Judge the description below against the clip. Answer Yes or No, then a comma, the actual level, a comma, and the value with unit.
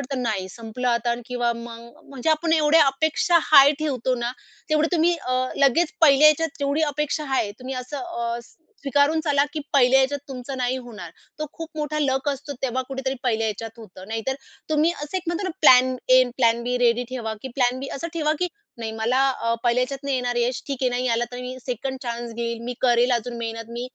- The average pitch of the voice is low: No, very high, 255 Hz